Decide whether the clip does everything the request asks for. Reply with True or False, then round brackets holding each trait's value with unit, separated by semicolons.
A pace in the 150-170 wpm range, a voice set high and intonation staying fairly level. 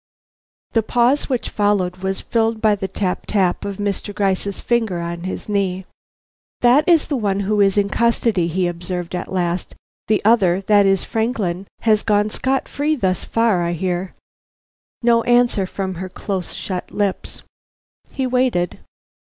False (160 wpm; 200 Hz; 3.7 semitones)